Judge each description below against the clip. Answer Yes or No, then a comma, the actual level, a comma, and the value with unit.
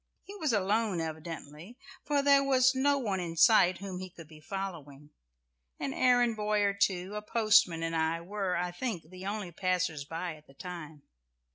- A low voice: No, medium, 185 Hz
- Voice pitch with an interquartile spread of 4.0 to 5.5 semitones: Yes, average, 5.0 semitones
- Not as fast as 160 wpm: No, average, 180 wpm